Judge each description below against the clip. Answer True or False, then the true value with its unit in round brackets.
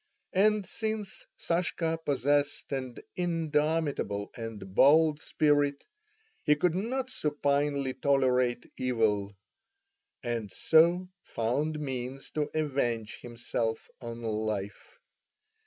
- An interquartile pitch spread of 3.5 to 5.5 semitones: True (5.2 semitones)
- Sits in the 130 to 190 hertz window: True (140 Hz)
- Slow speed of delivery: True (90 wpm)